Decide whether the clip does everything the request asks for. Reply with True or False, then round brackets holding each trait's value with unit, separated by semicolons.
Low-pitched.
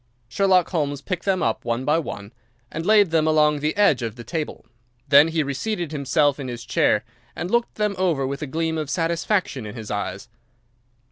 False (150 Hz)